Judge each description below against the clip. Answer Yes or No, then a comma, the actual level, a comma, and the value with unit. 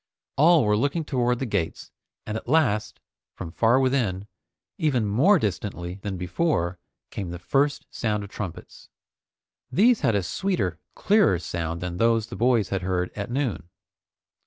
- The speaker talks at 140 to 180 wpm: Yes, average, 155 wpm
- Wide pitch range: Yes, wide, 6.8 semitones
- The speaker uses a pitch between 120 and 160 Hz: No, low, 110 Hz